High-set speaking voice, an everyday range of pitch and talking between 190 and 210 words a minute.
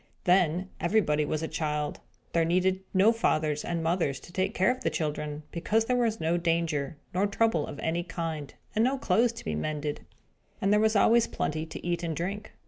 No: medium, 170 Hz; average, 4.9 semitones; average, 200 wpm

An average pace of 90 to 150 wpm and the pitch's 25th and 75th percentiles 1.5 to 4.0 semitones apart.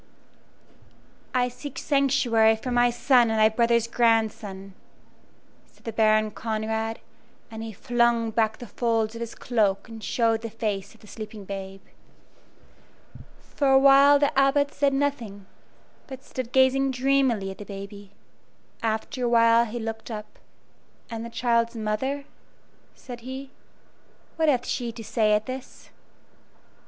Yes: average, 145 wpm; average, 2.9 semitones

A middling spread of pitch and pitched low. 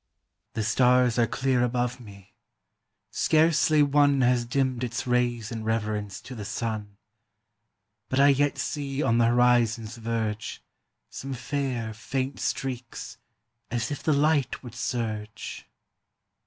Yes: average, 3.1 semitones; low, 125 Hz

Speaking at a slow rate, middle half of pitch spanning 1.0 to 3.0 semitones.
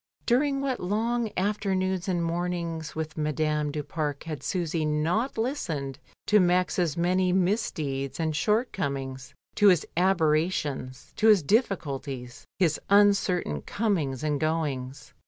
No: slow, 120 wpm; average, 4.6 semitones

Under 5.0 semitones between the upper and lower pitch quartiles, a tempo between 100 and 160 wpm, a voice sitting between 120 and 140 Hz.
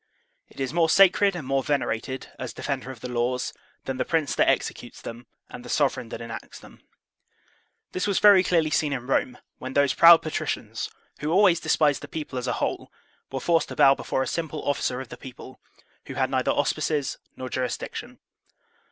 No: average, 4.1 semitones; average, 190 wpm; low, 135 Hz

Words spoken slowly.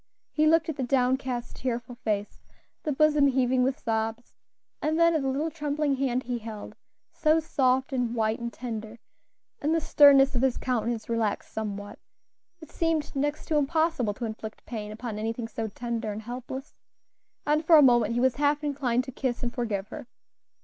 No: average, 180 wpm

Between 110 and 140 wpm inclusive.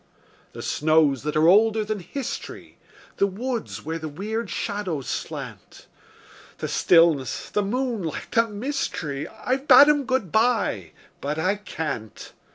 Yes: slow, 135 wpm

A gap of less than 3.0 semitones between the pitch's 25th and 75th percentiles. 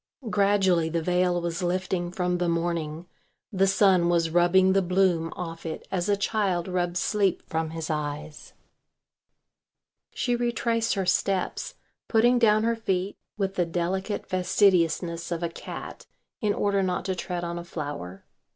Yes: narrow, 2.5 semitones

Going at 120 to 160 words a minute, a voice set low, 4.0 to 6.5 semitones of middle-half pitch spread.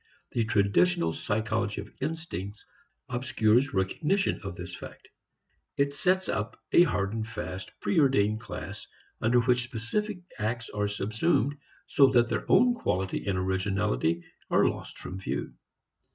Yes: slow, 135 wpm; low, 110 Hz; average, 5.1 semitones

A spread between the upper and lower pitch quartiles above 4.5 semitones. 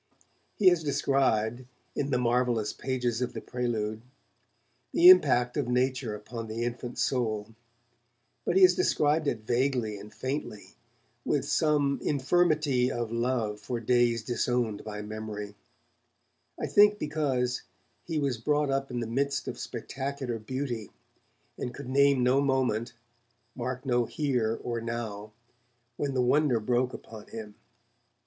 No: average, 3.4 semitones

